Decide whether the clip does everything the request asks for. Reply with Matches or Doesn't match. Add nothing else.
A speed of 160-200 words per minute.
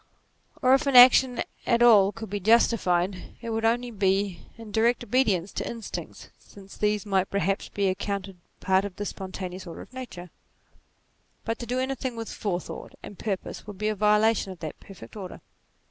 Matches